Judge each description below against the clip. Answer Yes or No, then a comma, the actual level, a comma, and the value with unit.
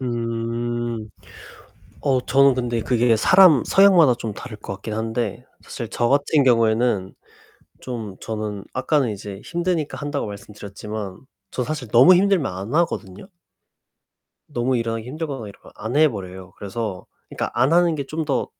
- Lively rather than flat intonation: No, average, 4.6 semitones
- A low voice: Yes, low, 120 Hz